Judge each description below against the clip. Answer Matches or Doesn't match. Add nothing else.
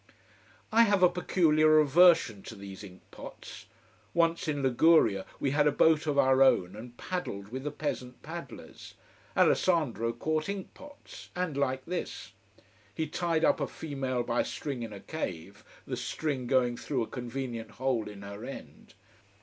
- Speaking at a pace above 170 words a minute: Doesn't match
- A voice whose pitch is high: Doesn't match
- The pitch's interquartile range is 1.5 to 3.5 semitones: Doesn't match